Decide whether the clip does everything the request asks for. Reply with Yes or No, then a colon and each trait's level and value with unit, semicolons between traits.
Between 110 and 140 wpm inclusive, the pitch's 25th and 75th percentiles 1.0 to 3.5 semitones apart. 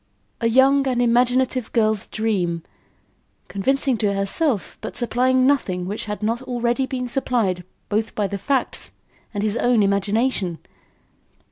No: slow, 135 wpm; average, 4.1 semitones